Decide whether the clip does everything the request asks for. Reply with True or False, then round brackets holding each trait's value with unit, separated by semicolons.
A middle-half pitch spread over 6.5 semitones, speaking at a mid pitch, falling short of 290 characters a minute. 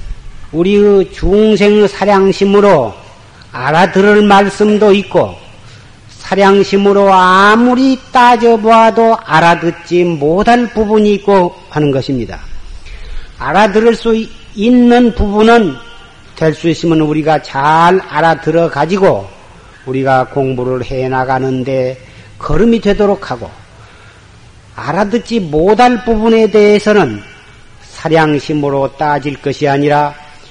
True (8.1 semitones; 165 Hz; 230 characters per minute)